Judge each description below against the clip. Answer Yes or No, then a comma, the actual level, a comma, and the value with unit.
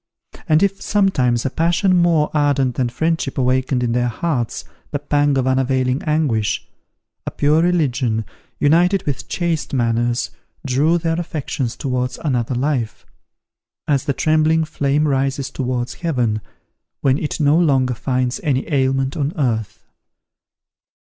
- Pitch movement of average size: Yes, average, 3.7 semitones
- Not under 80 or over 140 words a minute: Yes, slow, 135 wpm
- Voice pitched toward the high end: No, low, 135 Hz